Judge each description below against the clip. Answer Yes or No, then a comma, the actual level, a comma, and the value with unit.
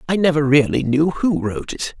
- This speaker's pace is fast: Yes, fast, 210 wpm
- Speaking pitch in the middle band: Yes, medium, 145 Hz